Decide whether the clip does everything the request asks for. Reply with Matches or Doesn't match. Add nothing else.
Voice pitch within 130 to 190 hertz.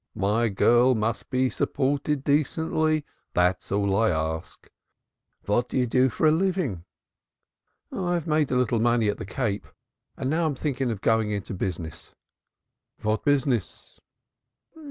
Doesn't match